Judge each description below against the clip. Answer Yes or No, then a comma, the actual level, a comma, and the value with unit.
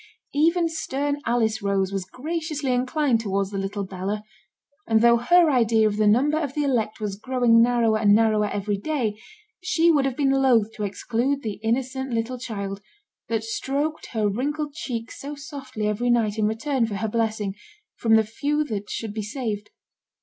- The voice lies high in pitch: Yes, high, 230 Hz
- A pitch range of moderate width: Yes, average, 4.5 semitones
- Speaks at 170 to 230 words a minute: Yes, average, 180 wpm